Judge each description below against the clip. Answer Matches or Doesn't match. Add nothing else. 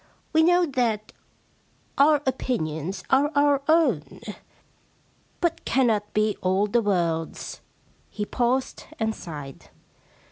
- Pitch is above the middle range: Matches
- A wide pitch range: Matches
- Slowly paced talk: Matches